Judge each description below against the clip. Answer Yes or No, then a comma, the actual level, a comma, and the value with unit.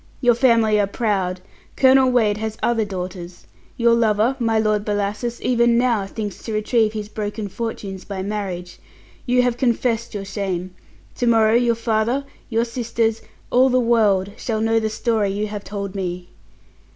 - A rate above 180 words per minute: No, average, 165 wpm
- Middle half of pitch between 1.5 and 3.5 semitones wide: Yes, narrow, 2.6 semitones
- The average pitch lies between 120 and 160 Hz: No, high, 220 Hz